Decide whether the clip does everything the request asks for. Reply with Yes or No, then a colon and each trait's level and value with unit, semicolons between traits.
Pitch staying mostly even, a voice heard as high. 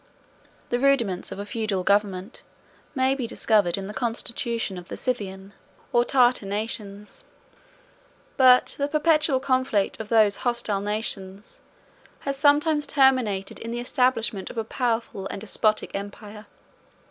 No: average, 4.2 semitones; high, 225 Hz